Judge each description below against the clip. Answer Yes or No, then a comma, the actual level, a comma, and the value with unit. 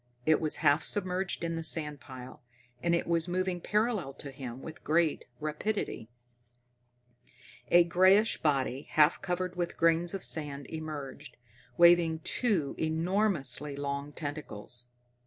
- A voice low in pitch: No, medium, 160 Hz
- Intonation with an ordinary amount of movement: Yes, average, 3.7 semitones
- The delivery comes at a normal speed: No, slow, 130 wpm